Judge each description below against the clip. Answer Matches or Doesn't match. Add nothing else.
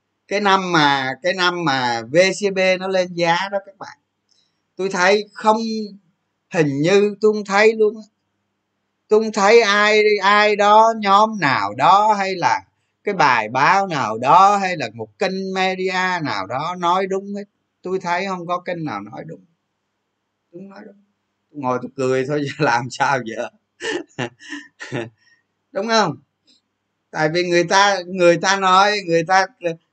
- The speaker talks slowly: Matches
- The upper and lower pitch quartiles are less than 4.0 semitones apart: Matches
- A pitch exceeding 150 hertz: Matches